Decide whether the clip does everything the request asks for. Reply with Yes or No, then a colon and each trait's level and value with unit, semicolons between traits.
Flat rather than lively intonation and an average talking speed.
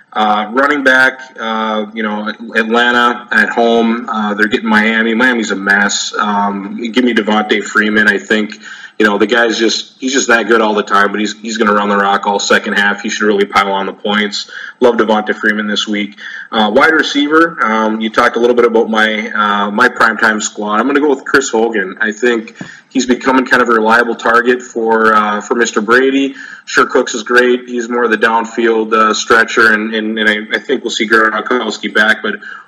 No: narrow, 2.2 semitones; fast, 215 wpm